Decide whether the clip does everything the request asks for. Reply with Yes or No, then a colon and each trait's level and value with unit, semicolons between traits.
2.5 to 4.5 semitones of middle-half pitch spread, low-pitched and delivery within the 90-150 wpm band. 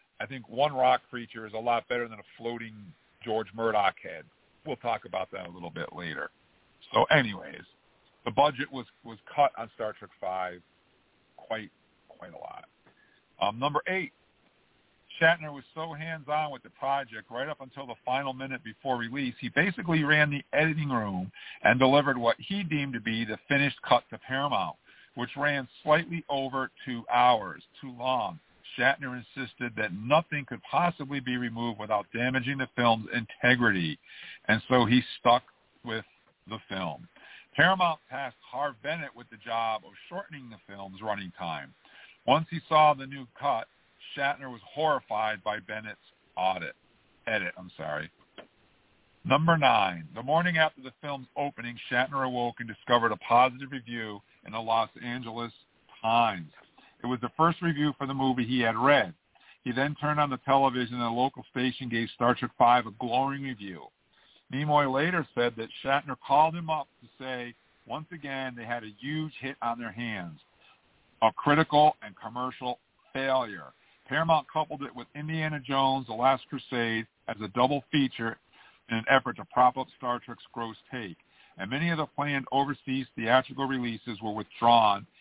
No: average, 3.6 semitones; low, 125 Hz; average, 165 wpm